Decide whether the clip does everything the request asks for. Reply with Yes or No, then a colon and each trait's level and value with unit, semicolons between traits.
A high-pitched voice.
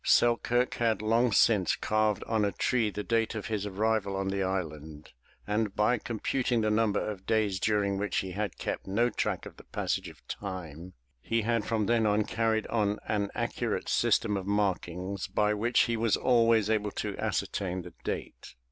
No: low, 105 Hz